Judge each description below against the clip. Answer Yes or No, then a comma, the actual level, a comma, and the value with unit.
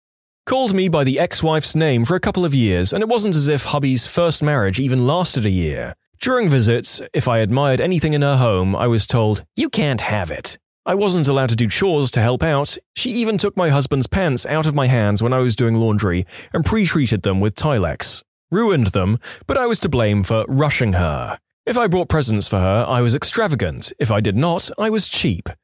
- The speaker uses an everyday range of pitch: No, wide, 6.9 semitones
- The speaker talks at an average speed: No, fast, 220 wpm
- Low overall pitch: Yes, low, 130 Hz